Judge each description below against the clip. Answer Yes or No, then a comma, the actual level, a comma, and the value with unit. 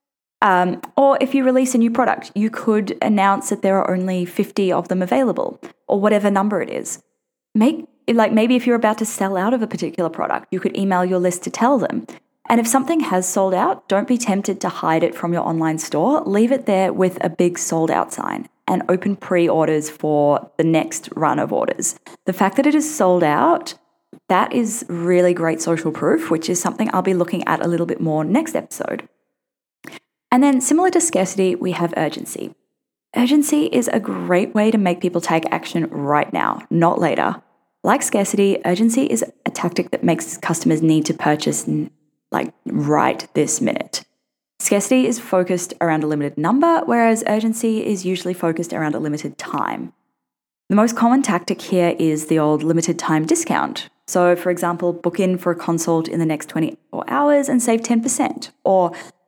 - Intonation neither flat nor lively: No, wide, 5.7 semitones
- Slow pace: No, average, 190 wpm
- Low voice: No, high, 190 Hz